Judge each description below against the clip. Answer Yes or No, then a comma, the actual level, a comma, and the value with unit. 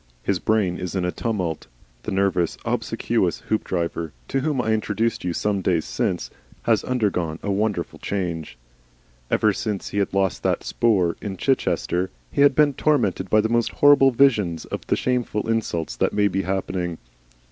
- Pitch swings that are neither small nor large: Yes, average, 4.3 semitones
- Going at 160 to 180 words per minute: Yes, average, 165 wpm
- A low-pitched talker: Yes, low, 100 Hz